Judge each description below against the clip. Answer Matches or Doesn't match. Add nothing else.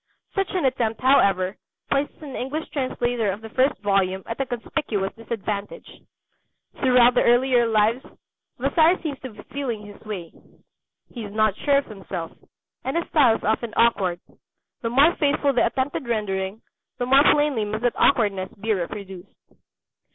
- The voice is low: Doesn't match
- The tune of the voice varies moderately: Matches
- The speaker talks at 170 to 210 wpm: Doesn't match